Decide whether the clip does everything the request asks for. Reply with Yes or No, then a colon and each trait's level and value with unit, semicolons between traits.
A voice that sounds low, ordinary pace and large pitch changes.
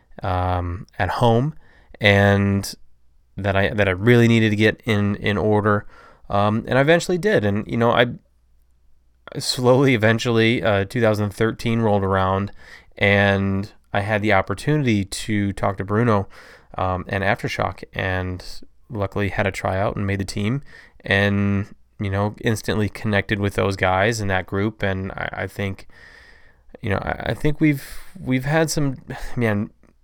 No: low, 105 Hz; average, 150 wpm; average, 3.0 semitones